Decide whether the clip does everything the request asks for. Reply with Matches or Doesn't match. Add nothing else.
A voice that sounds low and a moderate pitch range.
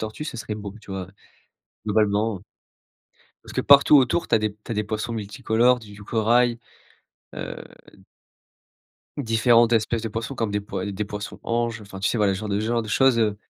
Doesn't match